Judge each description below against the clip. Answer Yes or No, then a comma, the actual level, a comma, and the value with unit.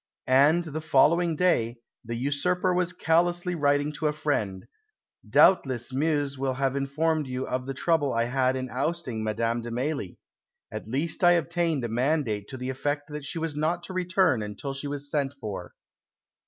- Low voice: No, medium, 145 Hz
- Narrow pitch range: No, average, 4.2 semitones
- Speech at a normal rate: Yes, average, 175 wpm